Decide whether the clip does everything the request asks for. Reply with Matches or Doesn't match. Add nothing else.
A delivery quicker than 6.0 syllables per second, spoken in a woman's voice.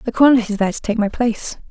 Matches